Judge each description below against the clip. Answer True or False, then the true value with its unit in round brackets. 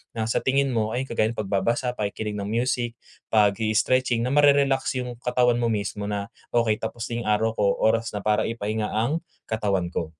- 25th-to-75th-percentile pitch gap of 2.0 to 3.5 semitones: True (2.7 semitones)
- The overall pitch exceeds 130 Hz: False (115 Hz)